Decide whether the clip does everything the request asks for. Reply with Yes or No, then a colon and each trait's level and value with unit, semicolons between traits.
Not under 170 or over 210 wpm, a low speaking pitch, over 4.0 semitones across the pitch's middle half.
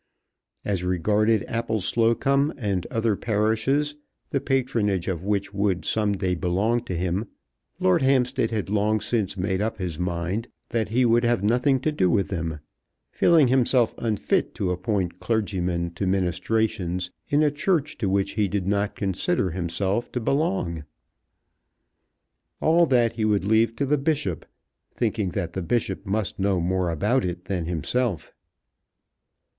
No: average, 150 wpm; low, 105 Hz; average, 4.4 semitones